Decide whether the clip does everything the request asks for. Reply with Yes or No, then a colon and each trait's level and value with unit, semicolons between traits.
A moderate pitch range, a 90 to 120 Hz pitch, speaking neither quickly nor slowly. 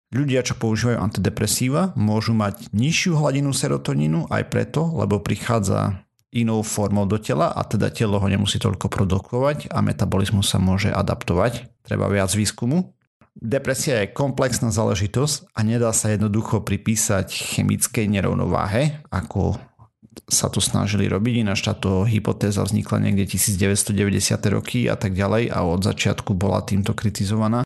Yes: average, 3.1 semitones; low, 110 Hz; average, 140 wpm